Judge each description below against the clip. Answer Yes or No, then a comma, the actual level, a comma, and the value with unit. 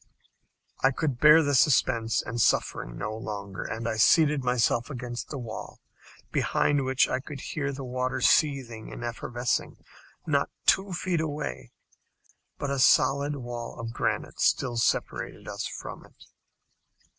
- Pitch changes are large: No, average, 3.5 semitones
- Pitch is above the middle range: No, low, 130 Hz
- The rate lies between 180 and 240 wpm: No, average, 140 wpm